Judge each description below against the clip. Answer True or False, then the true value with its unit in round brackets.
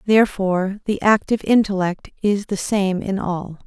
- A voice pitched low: False (200 Hz)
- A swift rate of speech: False (145 wpm)